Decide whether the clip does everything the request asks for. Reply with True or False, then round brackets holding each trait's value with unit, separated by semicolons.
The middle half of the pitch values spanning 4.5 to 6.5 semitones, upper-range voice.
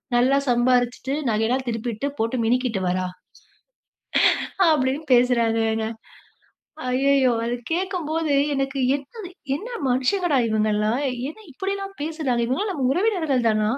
True (5.0 semitones; 260 Hz)